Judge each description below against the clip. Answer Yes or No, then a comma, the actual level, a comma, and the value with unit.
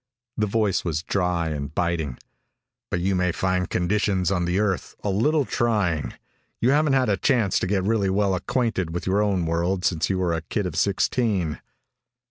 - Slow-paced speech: No, average, 185 wpm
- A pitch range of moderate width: Yes, average, 3.3 semitones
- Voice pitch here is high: No, very low, 95 Hz